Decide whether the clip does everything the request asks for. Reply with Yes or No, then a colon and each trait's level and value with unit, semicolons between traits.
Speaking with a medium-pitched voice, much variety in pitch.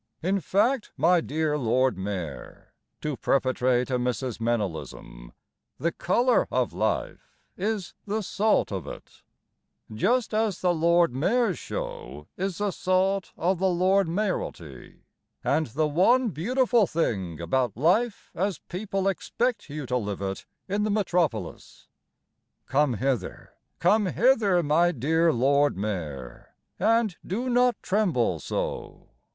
Yes: medium, 170 Hz; wide, 8.2 semitones